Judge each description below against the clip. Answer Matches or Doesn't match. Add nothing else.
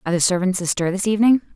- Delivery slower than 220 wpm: Doesn't match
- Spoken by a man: Doesn't match